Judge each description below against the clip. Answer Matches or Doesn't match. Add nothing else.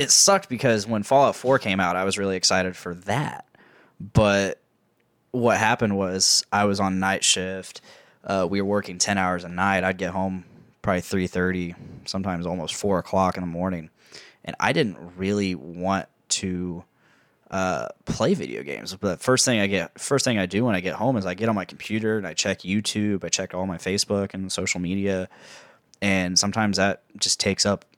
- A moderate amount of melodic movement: Doesn't match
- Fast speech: Doesn't match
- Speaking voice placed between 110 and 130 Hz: Doesn't match